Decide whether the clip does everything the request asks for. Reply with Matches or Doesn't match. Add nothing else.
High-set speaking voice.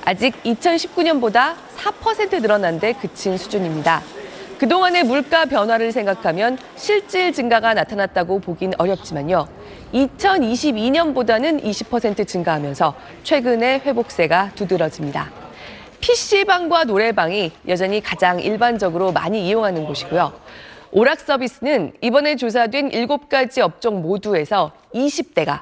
Matches